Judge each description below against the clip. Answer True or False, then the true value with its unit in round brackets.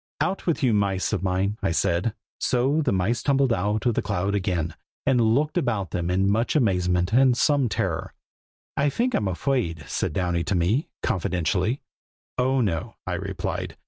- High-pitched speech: False (105 Hz)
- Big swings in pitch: True (6.1 semitones)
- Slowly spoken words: False (175 wpm)